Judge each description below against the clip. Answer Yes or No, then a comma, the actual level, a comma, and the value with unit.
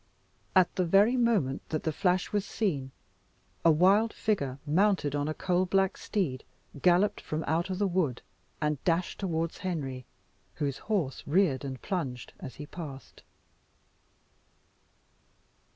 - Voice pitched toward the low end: No, medium, 170 Hz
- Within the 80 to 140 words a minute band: Yes, slow, 135 wpm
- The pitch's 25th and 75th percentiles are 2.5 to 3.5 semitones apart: No, average, 5.0 semitones